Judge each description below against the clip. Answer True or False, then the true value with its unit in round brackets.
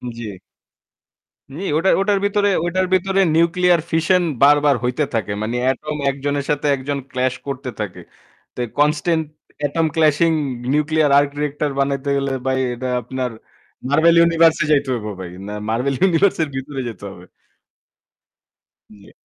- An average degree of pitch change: True (3.8 semitones)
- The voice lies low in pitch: False (145 Hz)